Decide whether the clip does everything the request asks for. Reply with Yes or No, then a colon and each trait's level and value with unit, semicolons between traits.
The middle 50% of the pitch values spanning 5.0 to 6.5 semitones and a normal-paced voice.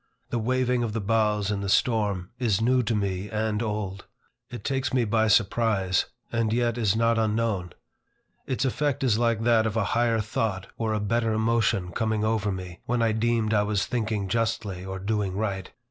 No: narrow, 2.4 semitones; average, 190 wpm